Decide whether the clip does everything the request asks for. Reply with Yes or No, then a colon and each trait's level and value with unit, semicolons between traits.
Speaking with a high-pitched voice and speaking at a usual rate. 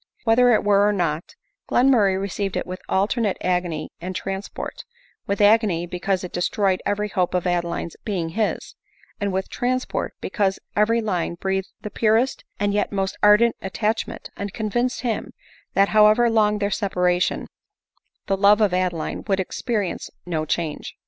Yes: high, 200 Hz; average, 160 wpm